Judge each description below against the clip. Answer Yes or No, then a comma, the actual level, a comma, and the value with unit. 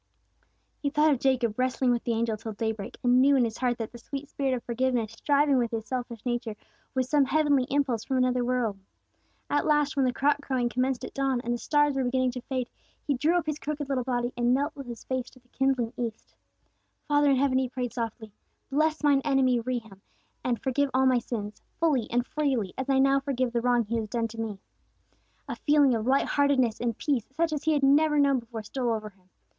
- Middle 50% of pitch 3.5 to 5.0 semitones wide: No, average, 2.9 semitones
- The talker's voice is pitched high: Yes, very high, 255 Hz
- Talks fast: Yes, fast, 225 wpm